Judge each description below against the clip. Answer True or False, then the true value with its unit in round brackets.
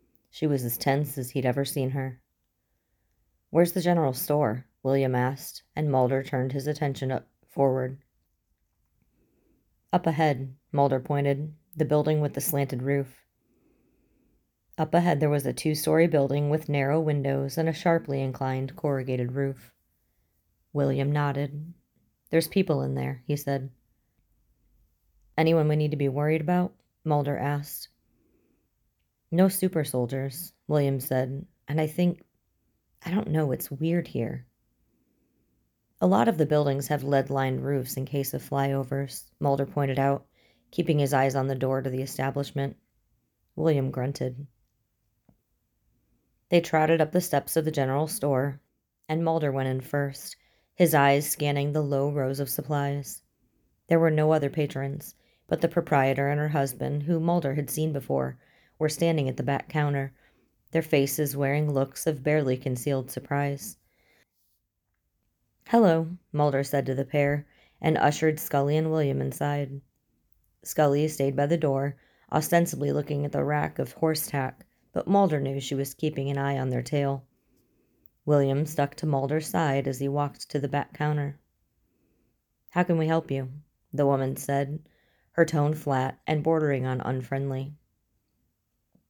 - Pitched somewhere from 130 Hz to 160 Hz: True (140 Hz)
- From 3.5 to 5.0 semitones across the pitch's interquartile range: False (2.4 semitones)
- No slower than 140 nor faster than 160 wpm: True (150 wpm)